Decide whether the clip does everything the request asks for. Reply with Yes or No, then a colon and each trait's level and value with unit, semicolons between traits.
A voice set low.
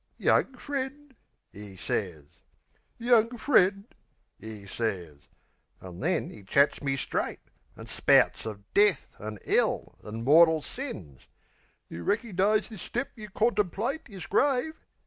No: high, 190 Hz